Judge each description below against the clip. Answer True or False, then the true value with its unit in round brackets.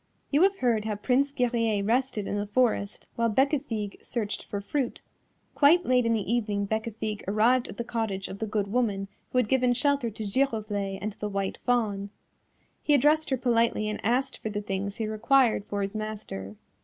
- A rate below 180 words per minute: False (190 wpm)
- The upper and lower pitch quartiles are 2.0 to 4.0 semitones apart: True (3.6 semitones)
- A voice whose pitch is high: True (220 Hz)